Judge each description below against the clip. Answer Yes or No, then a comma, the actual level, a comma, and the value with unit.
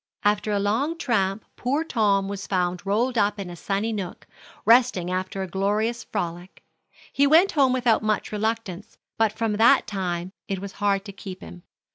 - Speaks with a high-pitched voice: Yes, high, 205 Hz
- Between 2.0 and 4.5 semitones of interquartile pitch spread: Yes, average, 3.0 semitones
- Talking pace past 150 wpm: Yes, average, 175 wpm